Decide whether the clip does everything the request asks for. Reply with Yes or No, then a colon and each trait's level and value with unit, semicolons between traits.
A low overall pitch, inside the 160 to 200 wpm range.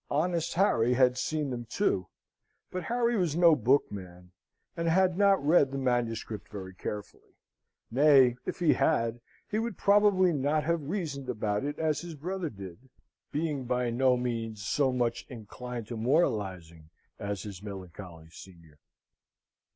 No: low, 125 Hz; average, 145 wpm